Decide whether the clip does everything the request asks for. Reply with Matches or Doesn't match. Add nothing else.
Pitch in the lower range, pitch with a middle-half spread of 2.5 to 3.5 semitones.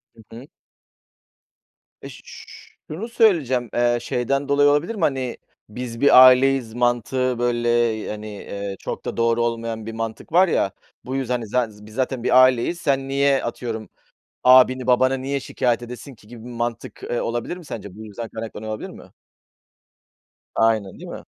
Matches